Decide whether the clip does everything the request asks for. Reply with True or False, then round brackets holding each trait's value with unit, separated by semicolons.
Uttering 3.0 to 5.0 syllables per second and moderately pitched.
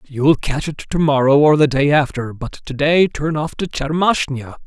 True (4.6 syllables/s; 145 Hz)